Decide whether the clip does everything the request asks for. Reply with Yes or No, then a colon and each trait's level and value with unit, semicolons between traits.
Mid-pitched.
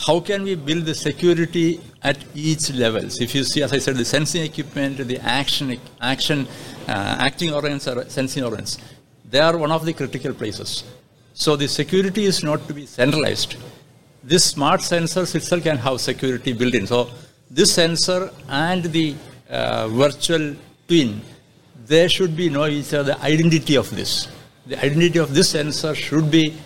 Yes: medium, 145 Hz